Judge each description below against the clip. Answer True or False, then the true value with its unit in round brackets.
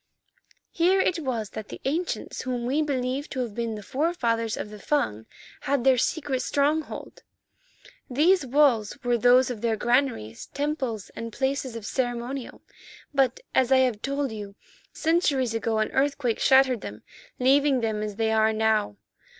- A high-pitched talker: True (250 Hz)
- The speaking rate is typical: True (160 wpm)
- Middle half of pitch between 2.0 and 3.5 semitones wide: False (4.0 semitones)